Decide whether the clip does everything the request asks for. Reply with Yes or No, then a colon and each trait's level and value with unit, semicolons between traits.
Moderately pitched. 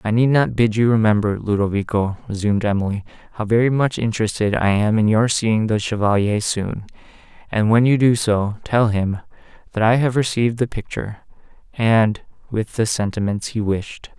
No: low, 110 Hz